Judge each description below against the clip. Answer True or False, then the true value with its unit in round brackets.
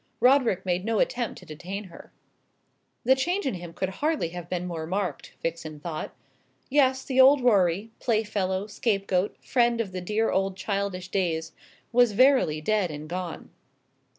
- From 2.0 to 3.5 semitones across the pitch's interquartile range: False (5.1 semitones)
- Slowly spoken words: False (155 wpm)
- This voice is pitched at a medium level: False (195 Hz)